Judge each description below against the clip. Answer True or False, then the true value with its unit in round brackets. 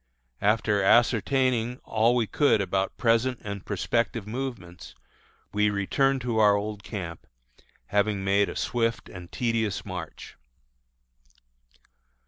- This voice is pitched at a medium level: False (110 Hz)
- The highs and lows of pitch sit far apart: False (3.0 semitones)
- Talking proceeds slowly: True (110 wpm)